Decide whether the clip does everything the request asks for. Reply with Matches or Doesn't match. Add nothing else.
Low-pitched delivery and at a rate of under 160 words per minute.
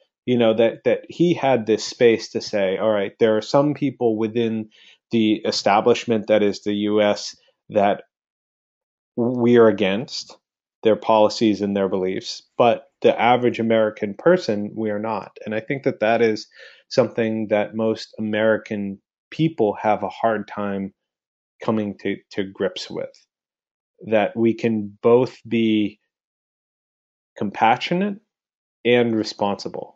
Matches